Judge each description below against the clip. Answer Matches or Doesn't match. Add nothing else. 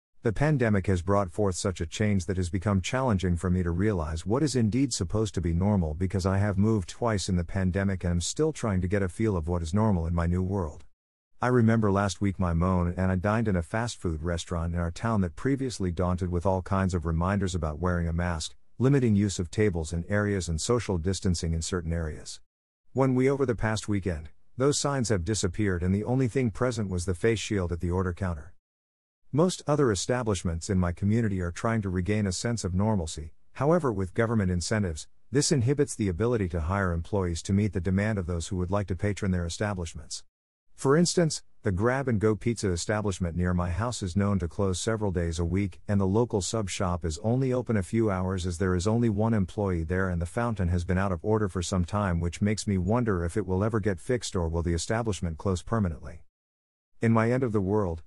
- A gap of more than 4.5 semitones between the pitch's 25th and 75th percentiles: Doesn't match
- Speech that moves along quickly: Matches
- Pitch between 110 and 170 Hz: Doesn't match